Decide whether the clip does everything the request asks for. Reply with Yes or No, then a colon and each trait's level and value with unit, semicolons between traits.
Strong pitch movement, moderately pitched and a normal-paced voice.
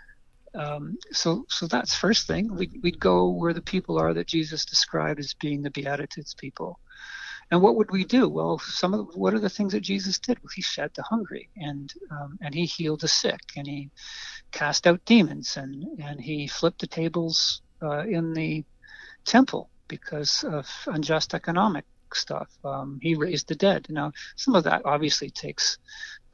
Yes: wide, 6.1 semitones; medium, 165 Hz; average, 180 wpm